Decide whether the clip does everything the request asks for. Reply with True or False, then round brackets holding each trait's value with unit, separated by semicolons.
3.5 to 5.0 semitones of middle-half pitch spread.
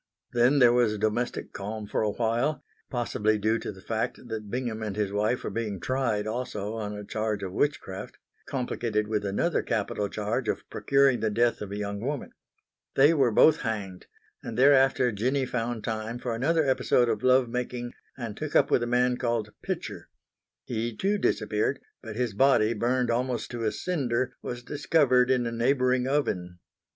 False (3.1 semitones)